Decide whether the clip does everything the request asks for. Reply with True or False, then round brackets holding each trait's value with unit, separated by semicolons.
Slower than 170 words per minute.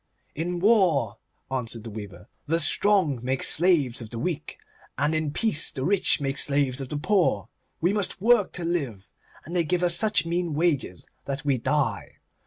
False (180 wpm)